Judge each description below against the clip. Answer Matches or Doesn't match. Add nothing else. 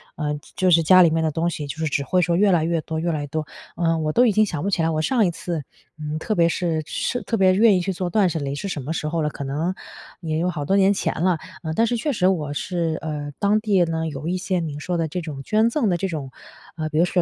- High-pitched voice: Doesn't match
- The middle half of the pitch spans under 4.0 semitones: Matches